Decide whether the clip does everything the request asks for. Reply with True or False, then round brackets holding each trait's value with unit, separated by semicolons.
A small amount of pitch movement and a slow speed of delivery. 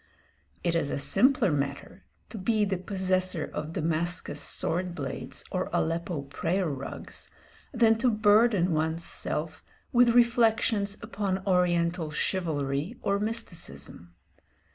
False (4.8 semitones; 120 wpm)